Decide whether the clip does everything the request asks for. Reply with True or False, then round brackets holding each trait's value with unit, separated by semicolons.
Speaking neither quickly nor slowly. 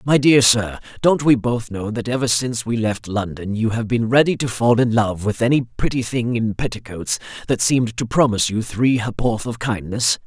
False (210 wpm)